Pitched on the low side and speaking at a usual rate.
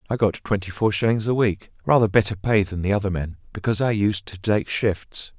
No: low, 100 Hz; fast, 225 wpm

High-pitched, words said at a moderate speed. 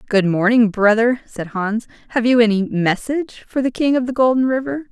Yes: high, 235 Hz; average, 195 wpm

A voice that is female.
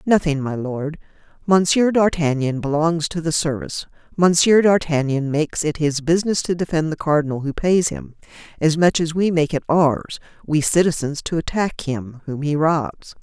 Yes: female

